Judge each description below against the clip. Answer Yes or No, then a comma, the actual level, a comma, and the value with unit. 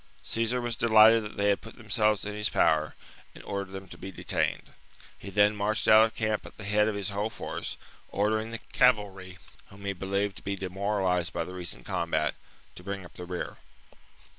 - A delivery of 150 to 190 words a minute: No, average, 200 wpm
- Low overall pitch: Yes, low, 100 Hz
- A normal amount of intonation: No, narrow, 2.2 semitones